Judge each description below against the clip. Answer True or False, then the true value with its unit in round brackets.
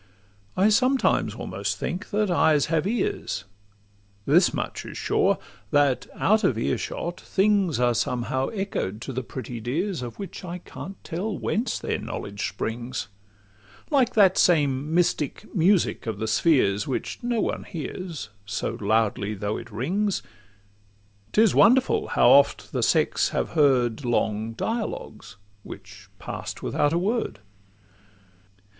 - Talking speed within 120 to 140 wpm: True (135 wpm)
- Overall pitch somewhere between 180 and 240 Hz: False (150 Hz)